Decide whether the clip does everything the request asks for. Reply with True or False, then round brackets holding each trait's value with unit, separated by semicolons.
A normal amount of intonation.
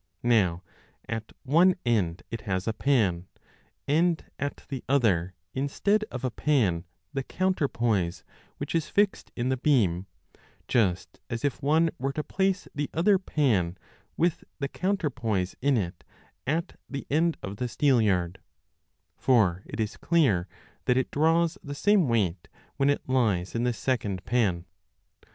False (7.3 semitones)